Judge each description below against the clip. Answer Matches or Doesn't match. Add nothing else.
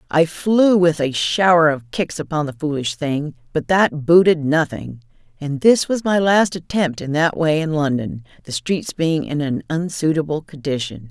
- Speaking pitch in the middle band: Matches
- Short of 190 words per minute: Matches